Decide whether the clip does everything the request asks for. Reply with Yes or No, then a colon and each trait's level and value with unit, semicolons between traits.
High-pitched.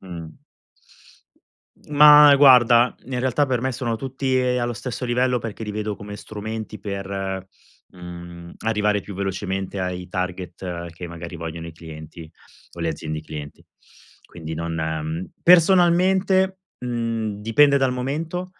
No: low, 105 Hz